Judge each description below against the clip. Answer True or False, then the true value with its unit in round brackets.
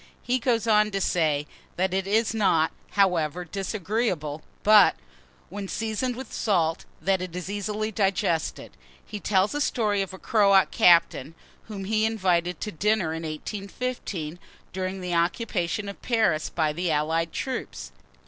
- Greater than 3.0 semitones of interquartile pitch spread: True (4.1 semitones)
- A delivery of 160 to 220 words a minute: False (150 wpm)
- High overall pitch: True (195 Hz)